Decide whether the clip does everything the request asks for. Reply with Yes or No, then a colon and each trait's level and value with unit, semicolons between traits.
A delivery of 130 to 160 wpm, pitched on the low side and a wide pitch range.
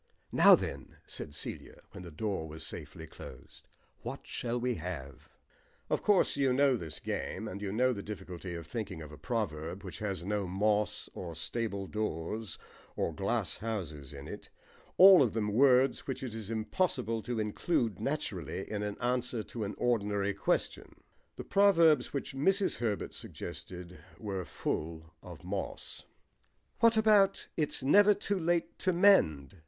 Yes: average, 155 wpm; low, 105 Hz; wide, 6.6 semitones